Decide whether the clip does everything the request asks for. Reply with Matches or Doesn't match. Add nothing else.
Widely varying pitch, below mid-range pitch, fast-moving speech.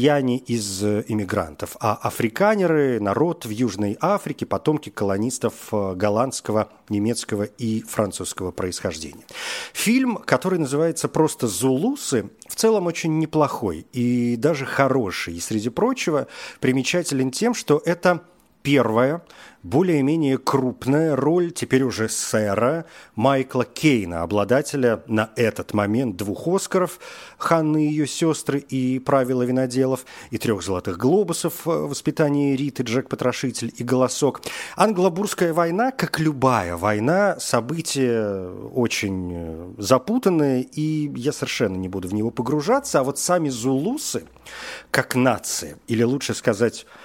Doesn't match